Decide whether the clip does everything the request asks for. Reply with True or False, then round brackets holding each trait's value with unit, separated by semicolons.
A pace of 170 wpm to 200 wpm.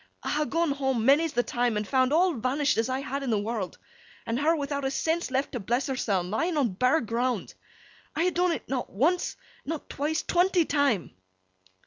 True (195 wpm)